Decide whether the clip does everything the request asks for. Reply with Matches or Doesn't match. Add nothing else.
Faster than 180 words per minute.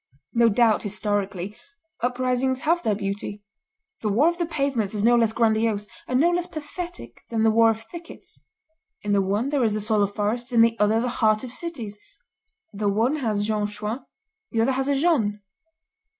Matches